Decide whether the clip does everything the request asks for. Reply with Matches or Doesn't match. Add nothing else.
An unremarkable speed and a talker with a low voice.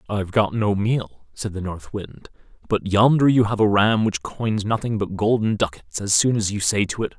Doesn't match